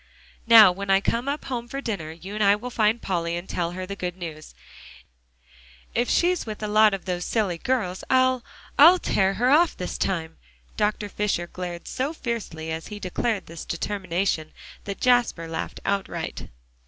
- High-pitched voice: Yes, high, 200 Hz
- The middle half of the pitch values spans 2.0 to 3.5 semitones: No, average, 4.9 semitones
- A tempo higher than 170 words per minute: Yes, average, 180 wpm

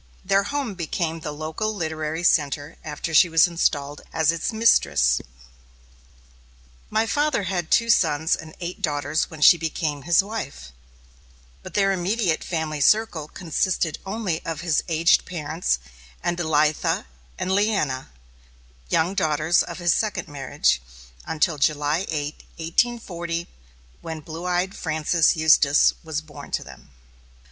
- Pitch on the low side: No, medium, 160 Hz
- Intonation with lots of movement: No, average, 3.1 semitones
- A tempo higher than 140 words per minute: No, slow, 135 wpm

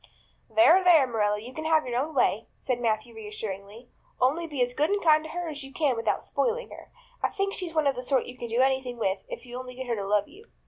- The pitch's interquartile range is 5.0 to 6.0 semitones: Yes, average, 5.3 semitones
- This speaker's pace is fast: Yes, fast, 270 wpm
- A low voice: No, very high, 255 Hz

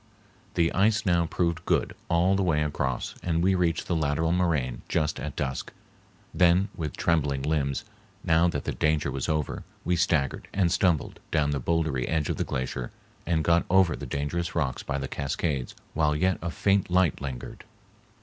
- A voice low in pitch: Yes, very low, 80 Hz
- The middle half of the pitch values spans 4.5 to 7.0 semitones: No, average, 3.3 semitones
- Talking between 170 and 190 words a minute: Yes, average, 180 wpm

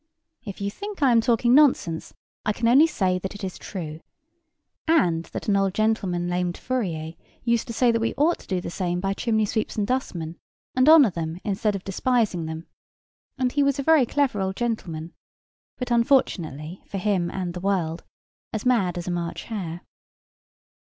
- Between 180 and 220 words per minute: Yes, average, 185 wpm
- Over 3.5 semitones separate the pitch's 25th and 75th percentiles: Yes, wide, 5.5 semitones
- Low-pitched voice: No, high, 200 Hz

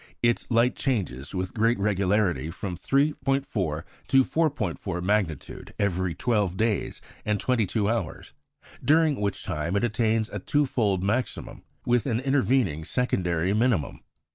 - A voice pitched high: No, low, 105 Hz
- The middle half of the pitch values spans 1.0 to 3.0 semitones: No, average, 5.2 semitones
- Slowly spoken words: Yes, slow, 130 wpm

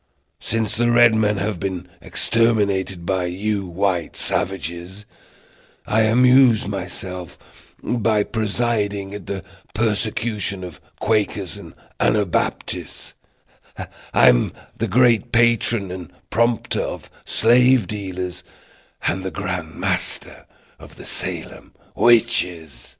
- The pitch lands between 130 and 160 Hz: No, low, 100 Hz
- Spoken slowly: Yes, slow, 105 wpm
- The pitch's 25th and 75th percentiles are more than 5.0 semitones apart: No, average, 3.6 semitones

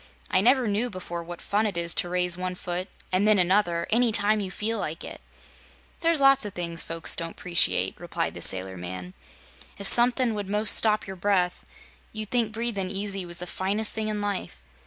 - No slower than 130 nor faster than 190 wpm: No, average, 200 wpm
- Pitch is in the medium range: No, high, 195 Hz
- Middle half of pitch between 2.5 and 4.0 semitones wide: Yes, average, 3.5 semitones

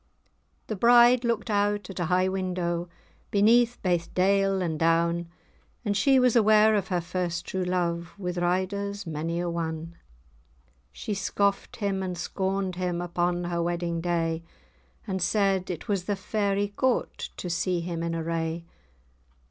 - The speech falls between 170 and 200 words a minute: No, average, 150 wpm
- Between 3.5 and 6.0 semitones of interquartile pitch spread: No, average, 2.8 semitones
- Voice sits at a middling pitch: Yes, medium, 180 Hz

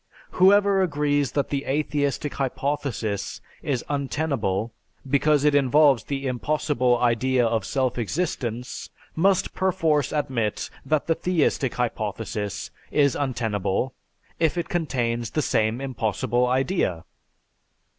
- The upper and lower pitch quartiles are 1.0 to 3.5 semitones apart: No, average, 4.1 semitones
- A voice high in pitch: No, low, 135 Hz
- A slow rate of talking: Yes, slow, 110 wpm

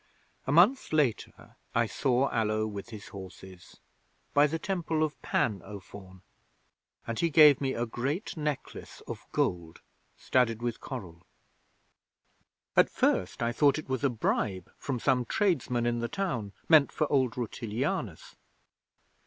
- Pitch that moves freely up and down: Yes, wide, 5.8 semitones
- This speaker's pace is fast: No, average, 145 wpm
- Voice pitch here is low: Yes, low, 120 Hz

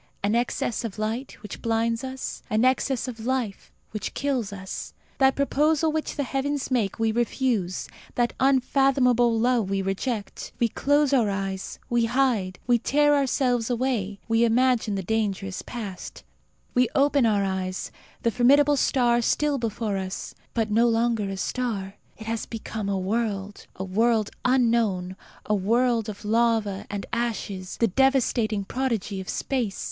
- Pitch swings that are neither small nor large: Yes, average, 4.0 semitones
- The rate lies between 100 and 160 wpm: Yes, average, 155 wpm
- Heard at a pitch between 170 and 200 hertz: No, high, 230 Hz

